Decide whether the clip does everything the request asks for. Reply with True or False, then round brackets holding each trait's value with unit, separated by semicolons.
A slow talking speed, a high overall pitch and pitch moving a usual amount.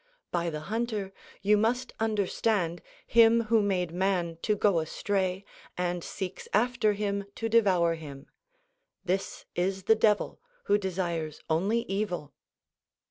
True (130 wpm; 195 Hz; 3.6 semitones)